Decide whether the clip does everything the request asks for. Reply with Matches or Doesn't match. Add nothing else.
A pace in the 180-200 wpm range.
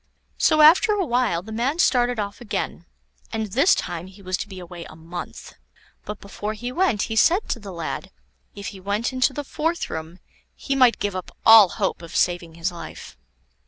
Matches